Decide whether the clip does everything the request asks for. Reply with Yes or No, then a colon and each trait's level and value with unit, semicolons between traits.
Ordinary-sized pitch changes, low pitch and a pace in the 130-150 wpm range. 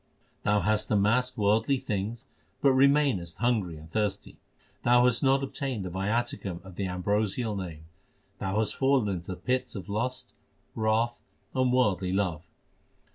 Yes: average, 4.6 semitones; low, 105 Hz; average, 145 wpm